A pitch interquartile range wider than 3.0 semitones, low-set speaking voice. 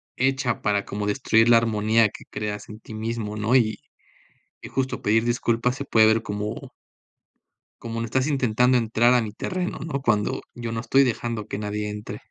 No: narrow, 2.6 semitones; low, 115 Hz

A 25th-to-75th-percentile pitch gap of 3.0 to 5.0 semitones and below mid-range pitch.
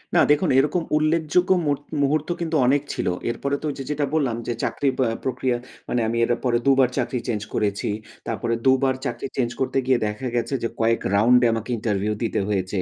Yes: average, 3.8 semitones; low, 130 Hz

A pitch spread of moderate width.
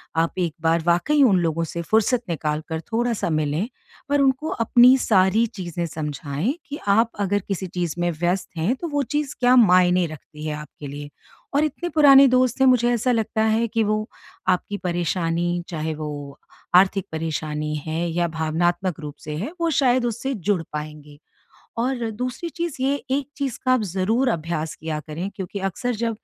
No: wide, 7.1 semitones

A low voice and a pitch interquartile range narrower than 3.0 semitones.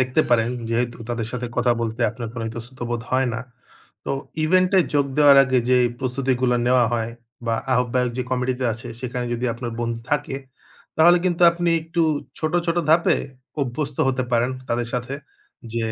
Yes: low, 125 Hz; narrow, 2.6 semitones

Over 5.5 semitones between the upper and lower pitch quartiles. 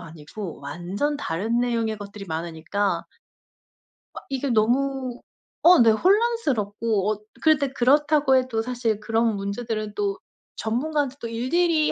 No: average, 5.2 semitones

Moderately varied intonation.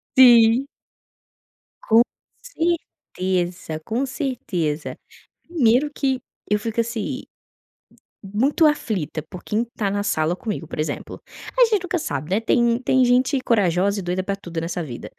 No: wide, 6.3 semitones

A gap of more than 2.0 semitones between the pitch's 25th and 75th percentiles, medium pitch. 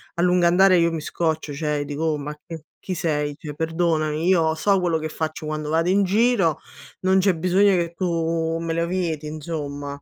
Yes: narrow, 2.5 semitones; medium, 165 Hz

